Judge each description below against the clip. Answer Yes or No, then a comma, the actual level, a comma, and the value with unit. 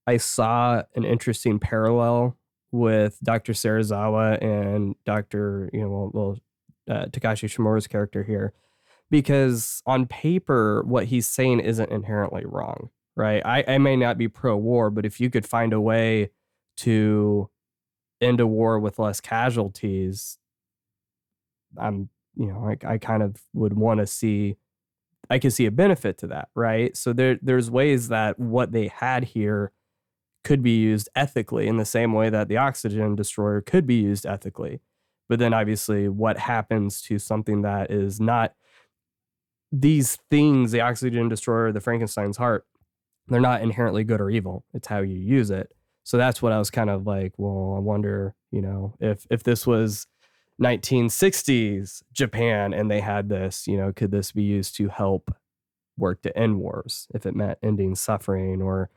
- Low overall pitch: Yes, low, 110 Hz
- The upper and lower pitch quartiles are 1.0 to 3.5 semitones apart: Yes, average, 2.8 semitones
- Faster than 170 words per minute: No, average, 165 wpm